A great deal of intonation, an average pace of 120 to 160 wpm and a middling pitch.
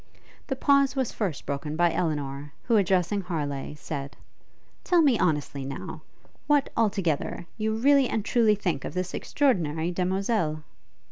Yes: wide, 6.9 semitones; average, 145 wpm; medium, 180 Hz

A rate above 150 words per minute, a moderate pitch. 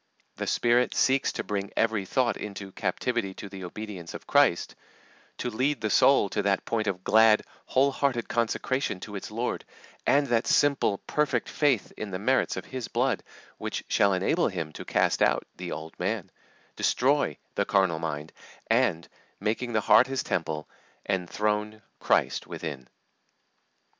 No: average, 160 wpm; low, 105 Hz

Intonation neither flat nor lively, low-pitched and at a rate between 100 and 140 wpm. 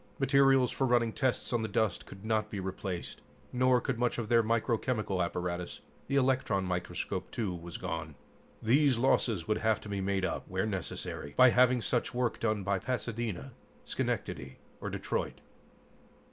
No: average, 4.6 semitones; low, 110 Hz; average, 160 wpm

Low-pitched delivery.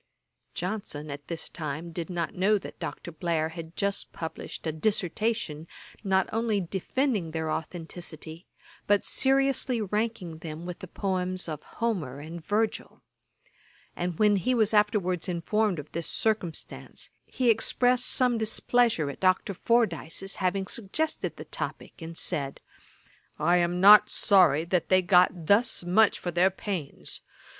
No: medium, 185 Hz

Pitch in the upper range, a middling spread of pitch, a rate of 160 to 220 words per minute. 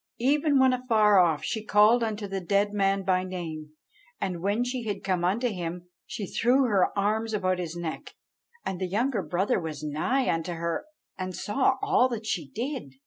Yes: high, 200 Hz; average, 4.7 semitones; average, 185 wpm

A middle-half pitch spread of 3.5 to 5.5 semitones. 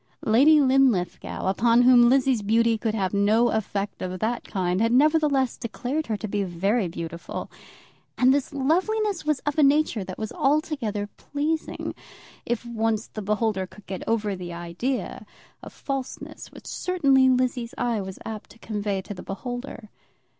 Yes: average, 4.8 semitones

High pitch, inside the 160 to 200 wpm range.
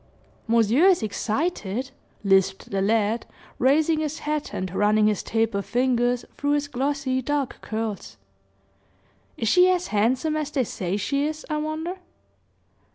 No: very high, 255 Hz; average, 140 wpm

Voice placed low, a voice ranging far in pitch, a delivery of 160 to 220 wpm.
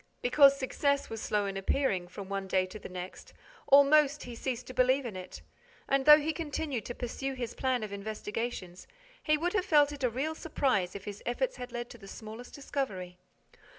No: high, 245 Hz; wide, 5.8 semitones; average, 195 wpm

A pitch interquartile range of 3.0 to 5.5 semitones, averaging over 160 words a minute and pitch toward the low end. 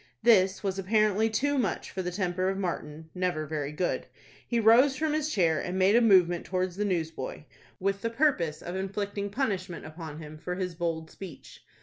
No: average, 3.8 semitones; average, 190 wpm; medium, 185 Hz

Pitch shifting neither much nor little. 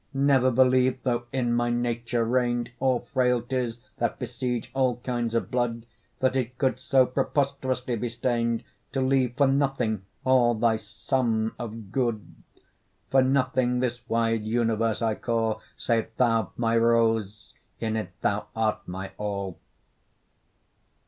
No: narrow, 2.1 semitones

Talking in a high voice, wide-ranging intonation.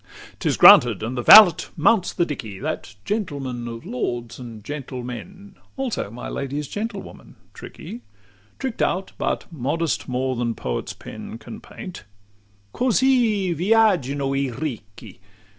No: medium, 140 Hz; wide, 8.1 semitones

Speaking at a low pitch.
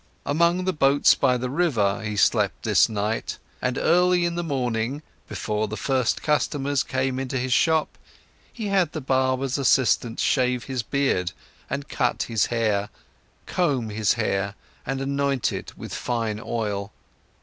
Yes: low, 130 Hz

